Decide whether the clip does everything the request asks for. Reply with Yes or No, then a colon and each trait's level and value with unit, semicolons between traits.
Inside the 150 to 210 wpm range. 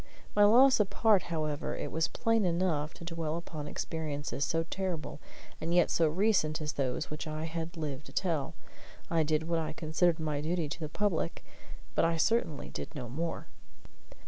Yes: average, 175 wpm